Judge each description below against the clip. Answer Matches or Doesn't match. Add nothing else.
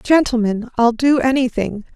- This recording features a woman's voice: Matches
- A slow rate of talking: Matches